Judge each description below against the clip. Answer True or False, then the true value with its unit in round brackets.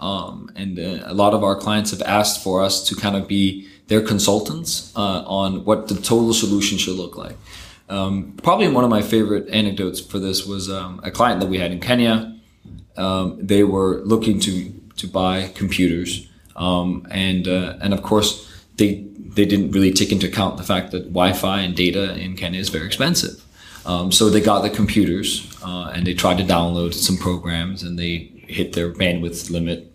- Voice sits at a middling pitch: False (95 Hz)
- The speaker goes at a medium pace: True (195 wpm)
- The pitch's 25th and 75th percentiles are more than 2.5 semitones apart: False (2.2 semitones)